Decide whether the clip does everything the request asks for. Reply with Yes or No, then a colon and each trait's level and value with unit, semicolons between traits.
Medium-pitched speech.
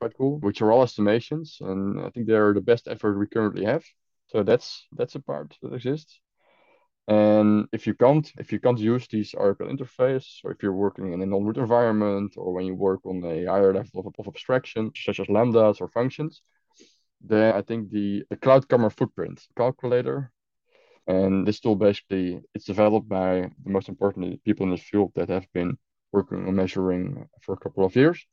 No: low, 105 Hz